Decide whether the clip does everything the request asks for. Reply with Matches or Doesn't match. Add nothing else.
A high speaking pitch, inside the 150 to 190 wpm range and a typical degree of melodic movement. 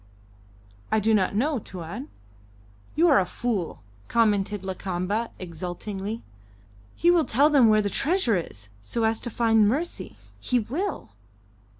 Doesn't match